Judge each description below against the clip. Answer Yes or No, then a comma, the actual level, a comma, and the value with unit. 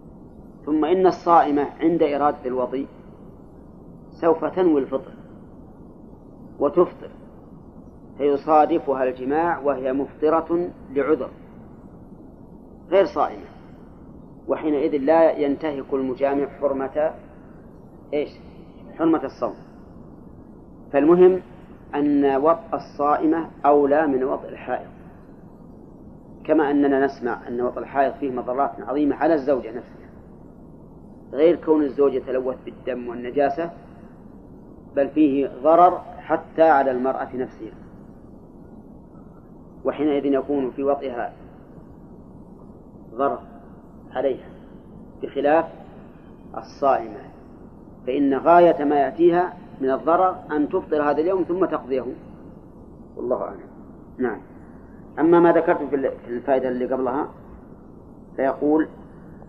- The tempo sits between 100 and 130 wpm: No, average, 90 wpm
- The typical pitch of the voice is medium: Yes, medium, 145 Hz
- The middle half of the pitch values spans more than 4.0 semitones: No, average, 3.7 semitones